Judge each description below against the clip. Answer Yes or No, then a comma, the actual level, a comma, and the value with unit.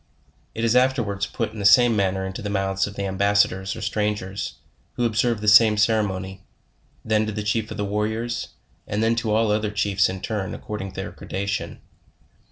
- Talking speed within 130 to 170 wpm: No, average, 200 wpm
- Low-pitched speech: Yes, low, 105 Hz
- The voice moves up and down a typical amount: No, narrow, 2.0 semitones